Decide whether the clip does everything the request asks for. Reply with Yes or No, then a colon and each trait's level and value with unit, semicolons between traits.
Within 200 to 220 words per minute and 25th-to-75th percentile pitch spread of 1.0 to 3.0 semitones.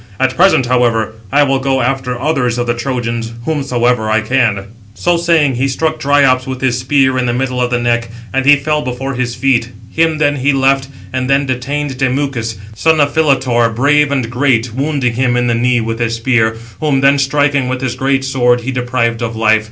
Yes: fast, 205 wpm; narrow, 2.4 semitones